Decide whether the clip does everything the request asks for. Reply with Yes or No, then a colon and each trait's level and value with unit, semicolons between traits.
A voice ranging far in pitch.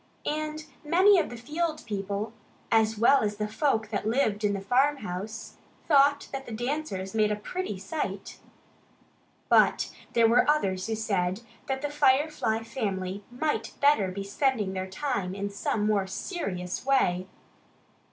Yes: wide, 6.0 semitones